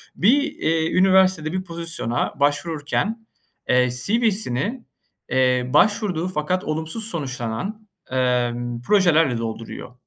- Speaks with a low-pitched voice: No, medium, 160 Hz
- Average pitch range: No, wide, 7.2 semitones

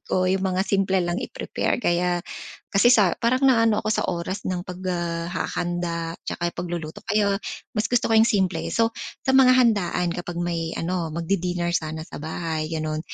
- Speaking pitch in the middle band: Yes, medium, 180 Hz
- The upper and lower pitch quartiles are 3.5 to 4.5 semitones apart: No, average, 3.1 semitones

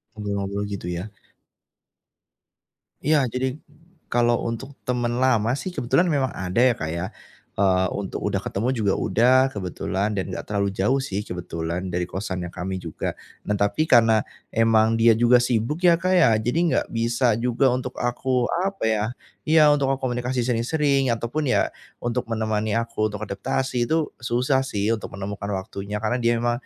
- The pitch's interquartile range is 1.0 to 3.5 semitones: No, average, 4.0 semitones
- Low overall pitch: Yes, low, 115 Hz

